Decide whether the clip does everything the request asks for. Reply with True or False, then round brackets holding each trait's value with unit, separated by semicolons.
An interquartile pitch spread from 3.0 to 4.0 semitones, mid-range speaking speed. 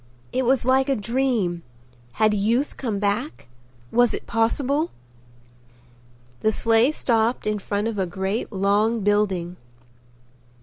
False (3.6 semitones; 125 wpm)